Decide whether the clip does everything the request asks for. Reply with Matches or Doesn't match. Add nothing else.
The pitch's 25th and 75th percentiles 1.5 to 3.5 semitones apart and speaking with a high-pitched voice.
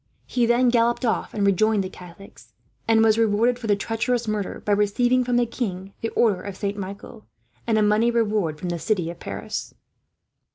Matches